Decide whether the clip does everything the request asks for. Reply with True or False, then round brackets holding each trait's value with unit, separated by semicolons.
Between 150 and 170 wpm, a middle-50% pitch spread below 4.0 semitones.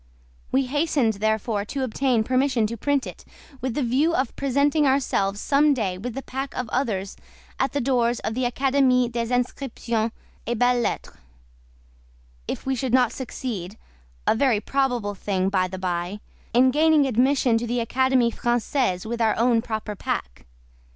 True (155 wpm; 3.5 semitones)